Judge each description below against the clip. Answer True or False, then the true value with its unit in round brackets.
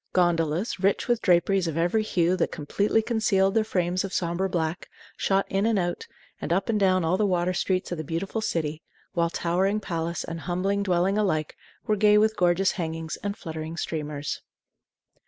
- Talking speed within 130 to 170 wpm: False (180 wpm)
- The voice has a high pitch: False (180 Hz)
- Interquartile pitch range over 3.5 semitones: False (3.1 semitones)